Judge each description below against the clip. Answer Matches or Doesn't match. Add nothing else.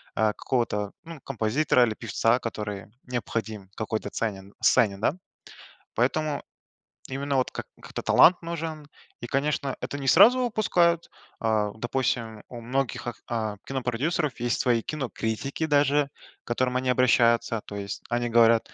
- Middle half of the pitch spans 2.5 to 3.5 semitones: Doesn't match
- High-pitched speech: Doesn't match